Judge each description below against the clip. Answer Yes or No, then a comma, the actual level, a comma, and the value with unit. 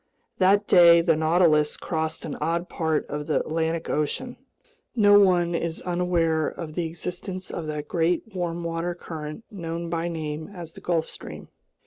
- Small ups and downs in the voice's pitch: Yes, narrow, 1.8 semitones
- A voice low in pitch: No, medium, 170 Hz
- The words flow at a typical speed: Yes, average, 160 wpm